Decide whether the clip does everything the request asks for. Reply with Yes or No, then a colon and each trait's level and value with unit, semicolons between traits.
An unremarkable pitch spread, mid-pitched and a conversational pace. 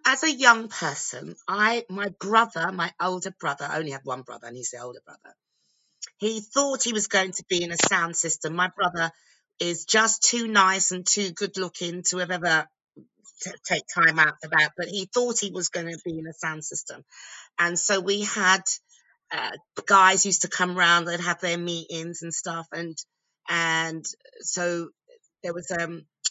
Yes: average, 3.3 semitones; medium, 180 Hz; average, 190 wpm